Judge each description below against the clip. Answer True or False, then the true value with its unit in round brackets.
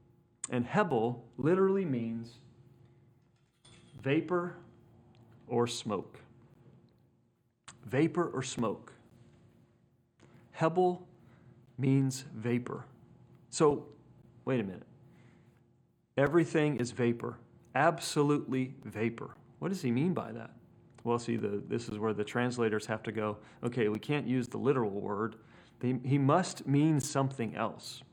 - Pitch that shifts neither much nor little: True (3.5 semitones)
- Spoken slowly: True (110 wpm)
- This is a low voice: True (125 Hz)